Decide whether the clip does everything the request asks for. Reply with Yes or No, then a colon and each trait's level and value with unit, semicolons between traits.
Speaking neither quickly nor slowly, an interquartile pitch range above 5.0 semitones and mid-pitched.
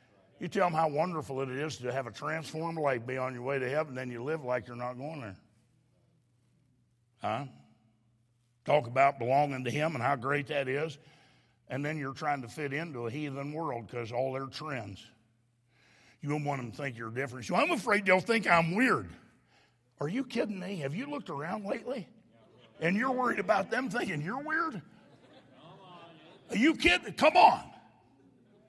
Yes: average, 185 wpm; wide, 5.4 semitones; medium, 145 Hz